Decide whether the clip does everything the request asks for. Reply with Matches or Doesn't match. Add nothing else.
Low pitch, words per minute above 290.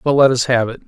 Matches